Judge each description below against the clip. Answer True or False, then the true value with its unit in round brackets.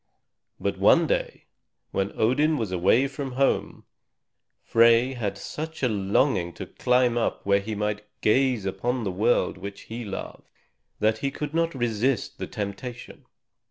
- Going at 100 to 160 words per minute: True (155 wpm)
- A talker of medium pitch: False (115 Hz)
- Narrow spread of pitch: False (4.7 semitones)